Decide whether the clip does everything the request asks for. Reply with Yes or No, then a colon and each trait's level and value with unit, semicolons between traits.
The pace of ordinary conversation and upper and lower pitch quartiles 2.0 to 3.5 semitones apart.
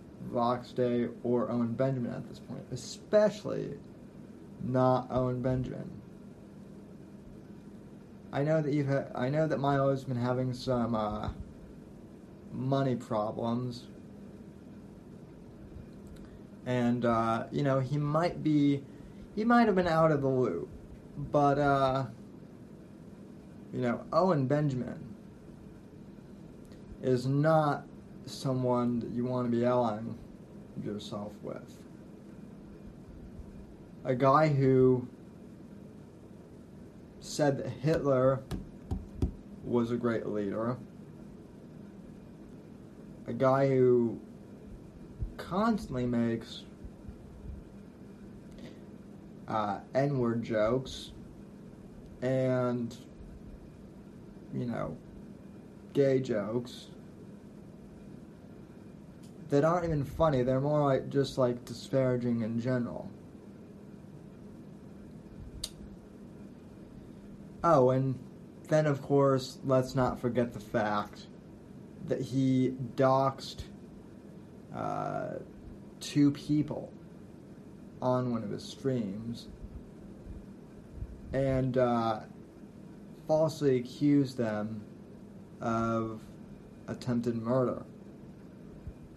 No: slow, 85 wpm; average, 2.8 semitones